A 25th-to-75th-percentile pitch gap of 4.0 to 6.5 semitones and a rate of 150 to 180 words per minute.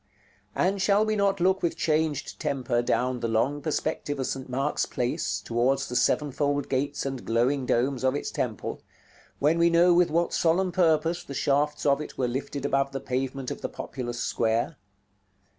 Yes: average, 4.3 semitones; average, 175 wpm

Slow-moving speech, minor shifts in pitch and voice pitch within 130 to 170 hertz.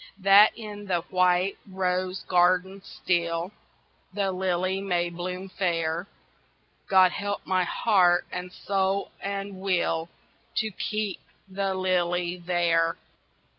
No: slow, 110 wpm; narrow, 1.8 semitones; medium, 185 Hz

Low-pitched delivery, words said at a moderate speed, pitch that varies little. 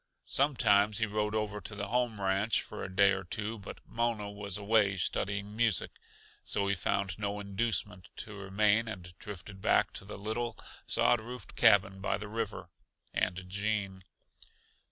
Yes: low, 105 Hz; average, 165 wpm; narrow, 2.0 semitones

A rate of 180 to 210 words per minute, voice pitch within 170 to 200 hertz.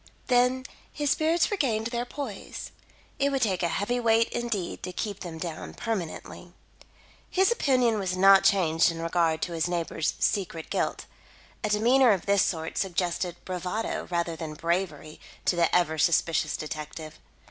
No: average, 155 wpm; medium, 185 Hz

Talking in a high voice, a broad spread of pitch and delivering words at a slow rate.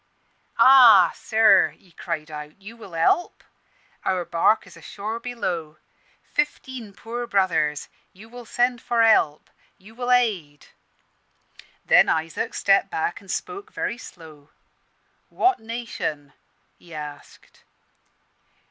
Yes: high, 200 Hz; wide, 6.4 semitones; slow, 110 wpm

